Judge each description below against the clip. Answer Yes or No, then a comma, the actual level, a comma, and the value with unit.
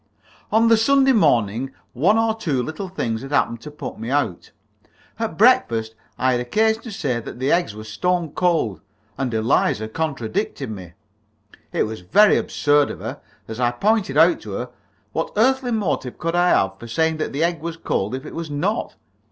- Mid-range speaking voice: Yes, medium, 145 Hz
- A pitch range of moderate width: No, wide, 7.5 semitones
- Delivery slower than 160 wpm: No, average, 190 wpm